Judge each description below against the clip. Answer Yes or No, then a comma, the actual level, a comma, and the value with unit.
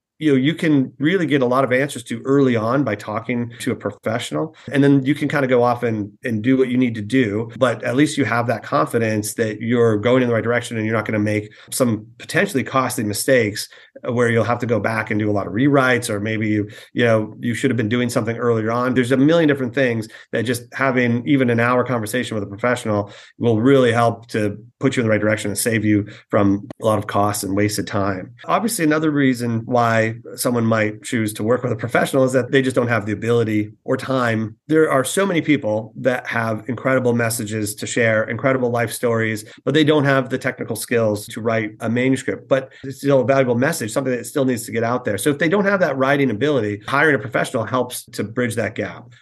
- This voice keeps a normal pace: No, fast, 240 wpm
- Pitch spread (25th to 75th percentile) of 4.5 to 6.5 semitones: No, average, 3.2 semitones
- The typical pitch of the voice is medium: No, low, 120 Hz